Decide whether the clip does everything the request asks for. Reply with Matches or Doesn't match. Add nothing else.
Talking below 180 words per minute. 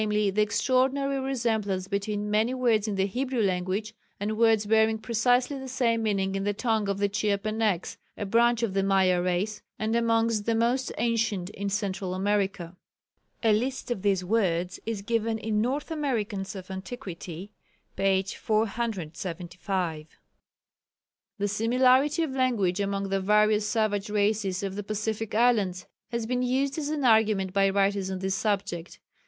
Matches